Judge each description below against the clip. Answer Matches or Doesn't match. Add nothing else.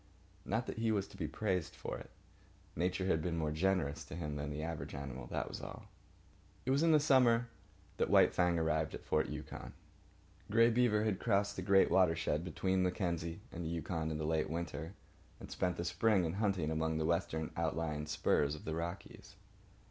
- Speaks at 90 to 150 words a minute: Doesn't match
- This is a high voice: Doesn't match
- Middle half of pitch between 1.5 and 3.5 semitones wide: Doesn't match